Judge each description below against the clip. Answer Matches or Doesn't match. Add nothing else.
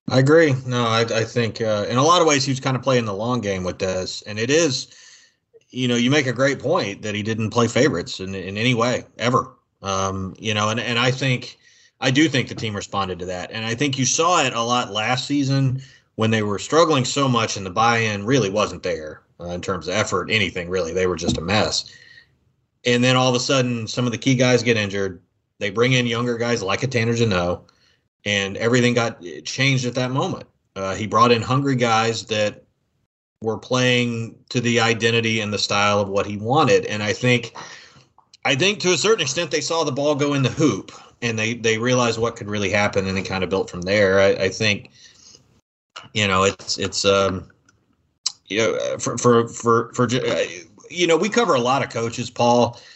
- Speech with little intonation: Doesn't match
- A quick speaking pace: Matches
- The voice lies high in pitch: Doesn't match